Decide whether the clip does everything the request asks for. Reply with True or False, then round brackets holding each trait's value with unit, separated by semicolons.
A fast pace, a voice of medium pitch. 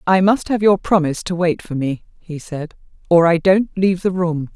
True (225 wpm; 175 Hz)